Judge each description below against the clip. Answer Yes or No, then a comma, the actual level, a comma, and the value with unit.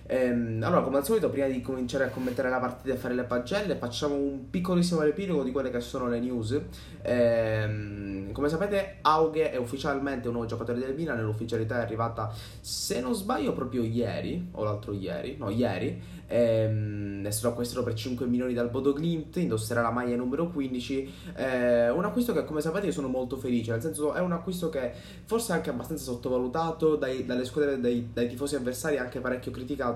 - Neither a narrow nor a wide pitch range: Yes, average, 3.8 semitones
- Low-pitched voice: Yes, low, 125 Hz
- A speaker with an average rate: No, fast, 190 wpm